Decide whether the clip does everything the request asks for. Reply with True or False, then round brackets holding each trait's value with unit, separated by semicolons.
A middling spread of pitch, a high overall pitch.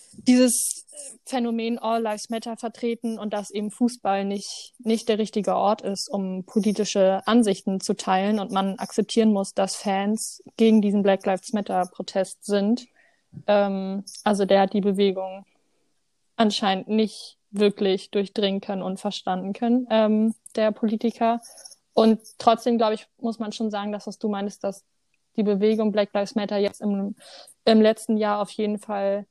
False (2.3 semitones; 210 Hz)